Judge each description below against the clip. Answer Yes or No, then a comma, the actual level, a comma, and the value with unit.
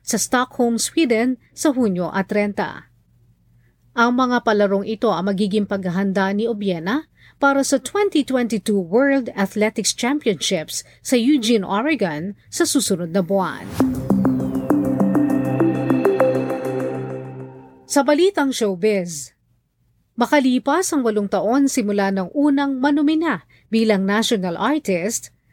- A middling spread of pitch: No, wide, 6.1 semitones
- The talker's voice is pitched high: Yes, high, 210 Hz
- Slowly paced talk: Yes, slow, 100 wpm